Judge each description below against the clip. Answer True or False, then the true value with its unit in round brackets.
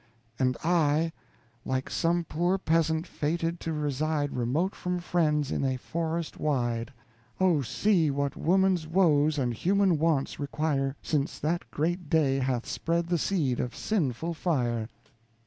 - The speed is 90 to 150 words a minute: True (140 wpm)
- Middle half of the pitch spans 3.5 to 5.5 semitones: True (3.8 semitones)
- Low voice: False (155 Hz)